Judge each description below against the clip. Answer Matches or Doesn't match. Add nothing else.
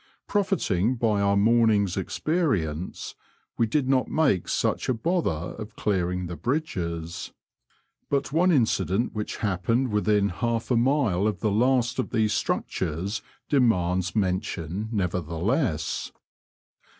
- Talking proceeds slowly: Matches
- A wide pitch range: Matches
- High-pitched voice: Doesn't match